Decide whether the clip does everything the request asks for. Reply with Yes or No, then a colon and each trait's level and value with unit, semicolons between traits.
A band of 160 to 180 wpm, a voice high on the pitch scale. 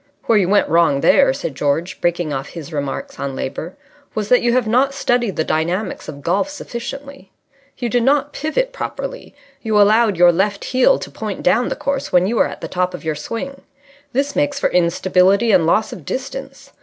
No: average, 200 wpm; high, 210 Hz